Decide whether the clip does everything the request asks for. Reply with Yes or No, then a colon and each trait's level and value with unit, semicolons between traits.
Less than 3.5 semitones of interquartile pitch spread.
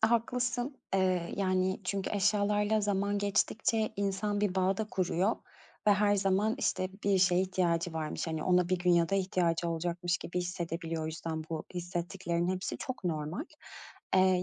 Yes: average, 2.8 semitones